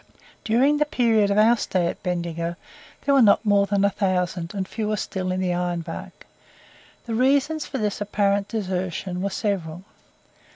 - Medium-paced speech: Yes, average, 170 wpm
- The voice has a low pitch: No, high, 200 Hz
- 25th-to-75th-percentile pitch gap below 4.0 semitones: Yes, average, 3.5 semitones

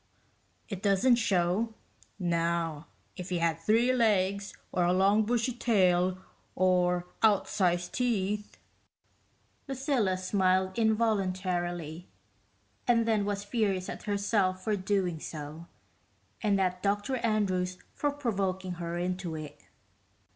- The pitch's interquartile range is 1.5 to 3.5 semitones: Yes, average, 3.2 semitones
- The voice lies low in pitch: No, high, 190 Hz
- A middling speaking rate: No, slow, 110 wpm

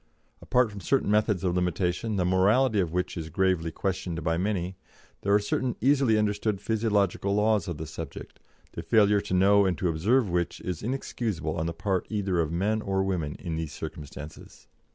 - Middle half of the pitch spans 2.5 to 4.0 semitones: Yes, average, 3.7 semitones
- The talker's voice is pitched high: No, very low, 95 Hz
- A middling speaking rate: Yes, average, 185 wpm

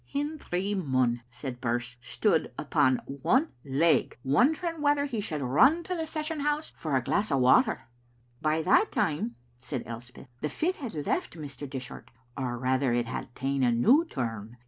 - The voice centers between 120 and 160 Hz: Yes, medium, 140 Hz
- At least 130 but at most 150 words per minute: No, average, 170 wpm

